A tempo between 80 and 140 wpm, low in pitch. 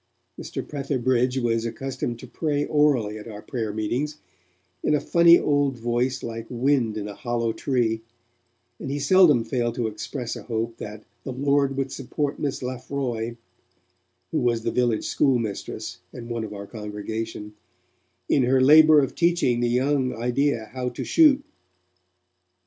No: average, 155 wpm; low, 125 Hz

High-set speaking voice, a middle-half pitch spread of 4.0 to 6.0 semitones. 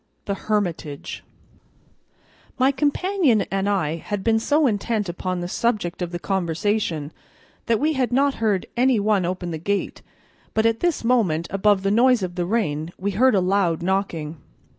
Yes: high, 200 Hz; average, 4.9 semitones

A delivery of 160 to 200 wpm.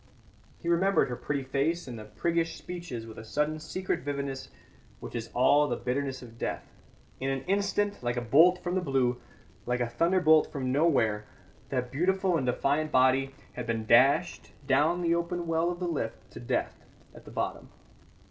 Yes: average, 175 wpm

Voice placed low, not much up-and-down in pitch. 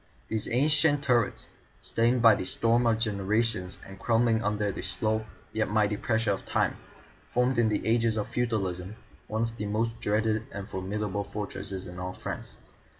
Yes: low, 110 Hz; narrow, 2.3 semitones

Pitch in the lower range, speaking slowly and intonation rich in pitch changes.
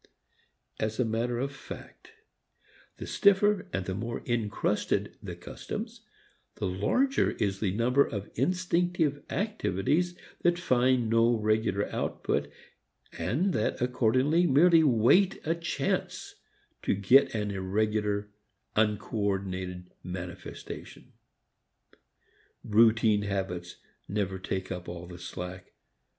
Yes: low, 110 Hz; slow, 105 wpm; wide, 6.4 semitones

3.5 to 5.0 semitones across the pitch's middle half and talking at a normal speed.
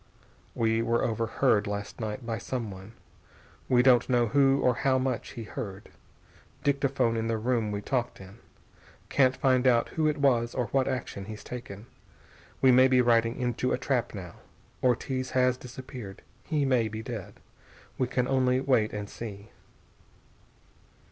No: average, 2.7 semitones; average, 155 wpm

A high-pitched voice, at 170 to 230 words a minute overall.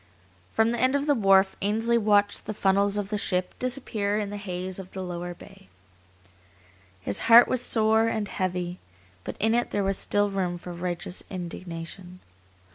Yes: high, 200 Hz; average, 175 wpm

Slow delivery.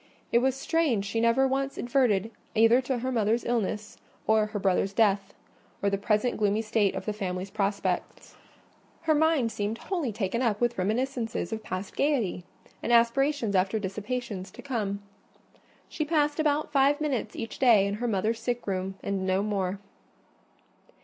No: average, 165 wpm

